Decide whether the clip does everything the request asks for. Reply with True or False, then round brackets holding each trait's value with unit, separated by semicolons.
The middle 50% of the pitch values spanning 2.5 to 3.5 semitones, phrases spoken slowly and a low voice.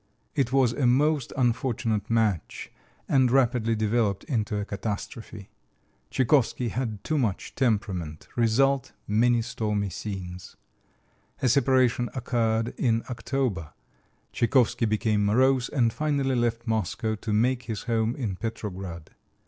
True (3.2 semitones; 120 wpm; 115 Hz)